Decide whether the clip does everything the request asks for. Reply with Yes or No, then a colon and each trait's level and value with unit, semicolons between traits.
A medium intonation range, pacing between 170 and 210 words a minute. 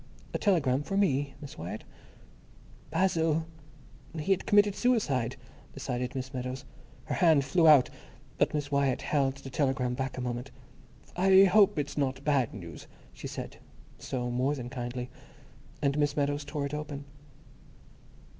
No: average, 3.2 semitones; average, 145 wpm